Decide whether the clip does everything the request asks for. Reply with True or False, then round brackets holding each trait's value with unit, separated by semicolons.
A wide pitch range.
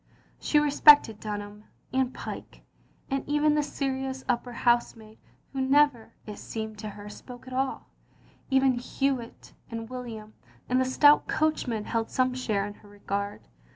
False (3.8 semitones)